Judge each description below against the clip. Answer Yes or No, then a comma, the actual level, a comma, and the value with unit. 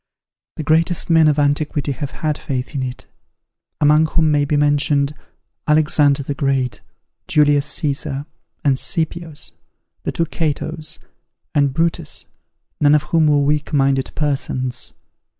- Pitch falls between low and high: Yes, medium, 145 Hz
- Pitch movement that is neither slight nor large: No, narrow, 1.8 semitones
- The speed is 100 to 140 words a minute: Yes, slow, 135 wpm